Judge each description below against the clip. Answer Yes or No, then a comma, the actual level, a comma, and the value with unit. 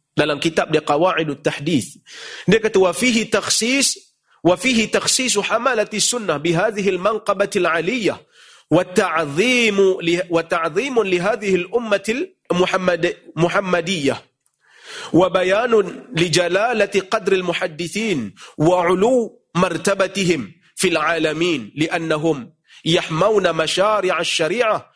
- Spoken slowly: Yes, slow, 75 wpm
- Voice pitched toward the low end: No, medium, 185 Hz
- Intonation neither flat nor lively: Yes, average, 3.8 semitones